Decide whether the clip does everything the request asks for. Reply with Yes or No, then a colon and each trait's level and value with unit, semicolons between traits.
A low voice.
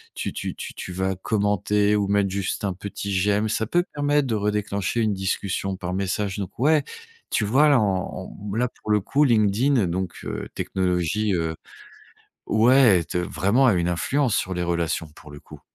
Yes: low, 100 Hz